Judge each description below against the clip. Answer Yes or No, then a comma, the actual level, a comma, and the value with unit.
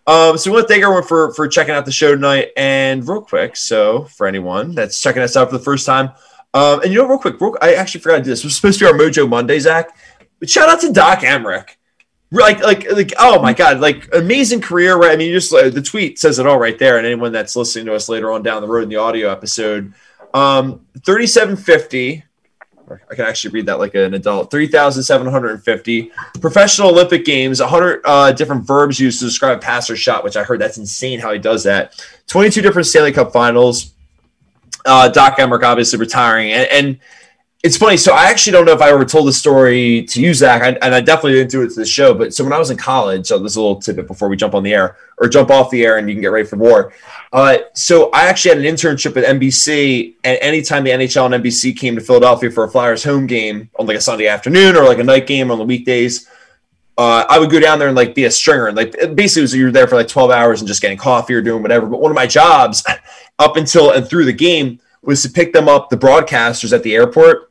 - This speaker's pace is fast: Yes, fast, 250 wpm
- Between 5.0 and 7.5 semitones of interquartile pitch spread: Yes, wide, 5.5 semitones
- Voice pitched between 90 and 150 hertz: Yes, low, 135 Hz